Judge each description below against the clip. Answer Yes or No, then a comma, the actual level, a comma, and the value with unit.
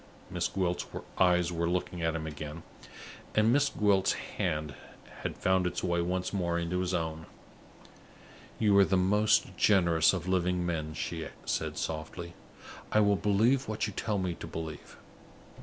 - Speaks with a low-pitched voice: Yes, very low, 90 Hz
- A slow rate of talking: No, average, 155 wpm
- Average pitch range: Yes, average, 3.0 semitones